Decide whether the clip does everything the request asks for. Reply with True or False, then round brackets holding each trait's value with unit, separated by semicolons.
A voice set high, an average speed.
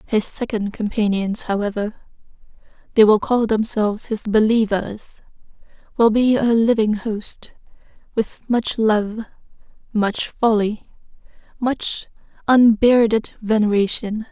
False (220 Hz; 90 wpm)